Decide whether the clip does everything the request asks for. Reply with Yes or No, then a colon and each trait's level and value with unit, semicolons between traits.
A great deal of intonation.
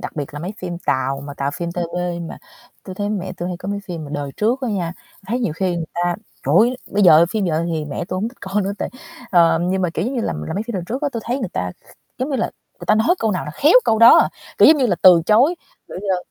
No: average, 4.6 semitones